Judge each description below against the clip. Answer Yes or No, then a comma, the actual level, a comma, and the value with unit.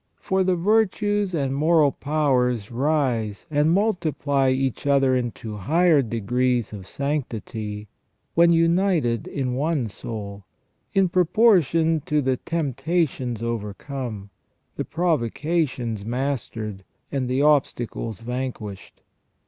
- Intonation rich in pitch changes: Yes, wide, 5.7 semitones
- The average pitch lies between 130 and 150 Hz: Yes, low, 135 Hz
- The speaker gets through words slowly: Yes, slow, 105 wpm